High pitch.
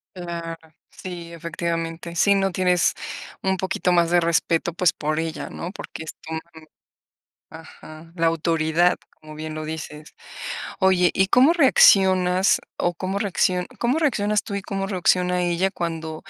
No: medium, 175 Hz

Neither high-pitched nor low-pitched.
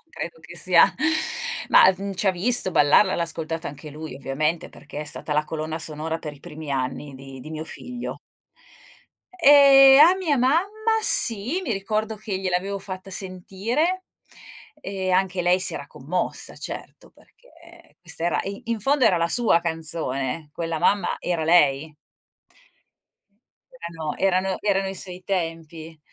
Yes: medium, 180 Hz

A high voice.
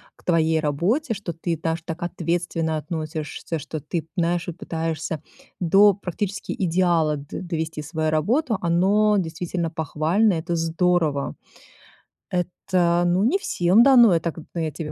No: medium, 170 Hz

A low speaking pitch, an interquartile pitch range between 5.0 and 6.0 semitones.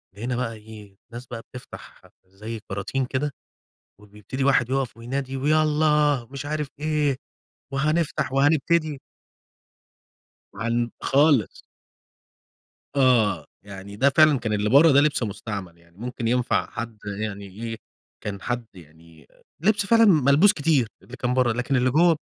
Yes: low, 125 Hz; average, 5.3 semitones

